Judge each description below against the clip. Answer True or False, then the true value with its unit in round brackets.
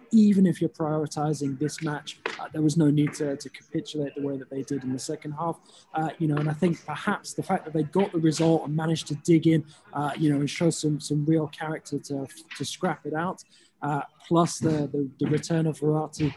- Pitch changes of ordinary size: False (1.9 semitones)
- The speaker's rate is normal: False (235 wpm)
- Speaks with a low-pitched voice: False (155 Hz)